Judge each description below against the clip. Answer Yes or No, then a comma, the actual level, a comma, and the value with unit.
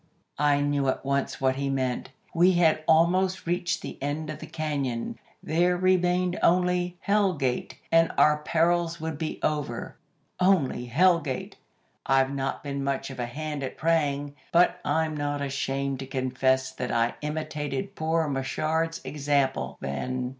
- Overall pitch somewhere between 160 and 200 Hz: No, medium, 150 Hz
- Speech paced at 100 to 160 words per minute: Yes, average, 155 wpm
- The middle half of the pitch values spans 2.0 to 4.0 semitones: Yes, average, 3.6 semitones